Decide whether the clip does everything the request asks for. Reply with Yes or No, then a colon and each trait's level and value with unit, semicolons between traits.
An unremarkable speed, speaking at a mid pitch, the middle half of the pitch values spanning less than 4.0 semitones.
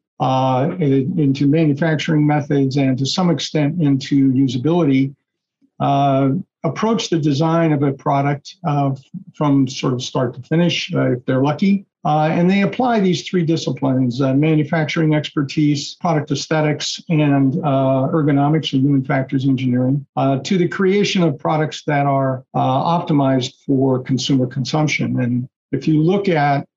Yes: average, 145 wpm; medium, 145 Hz; average, 3.2 semitones